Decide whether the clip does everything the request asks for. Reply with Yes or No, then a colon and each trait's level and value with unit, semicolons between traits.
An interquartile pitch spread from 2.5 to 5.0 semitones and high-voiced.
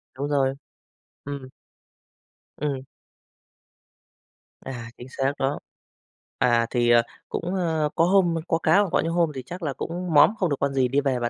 No: average, 4.0 semitones; medium, 145 Hz